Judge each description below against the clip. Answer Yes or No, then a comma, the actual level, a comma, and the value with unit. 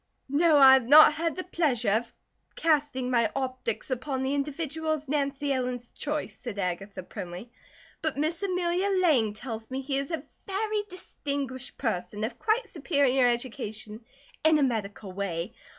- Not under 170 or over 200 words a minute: No, average, 155 wpm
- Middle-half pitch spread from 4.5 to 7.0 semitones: Yes, average, 5.0 semitones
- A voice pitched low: No, very high, 270 Hz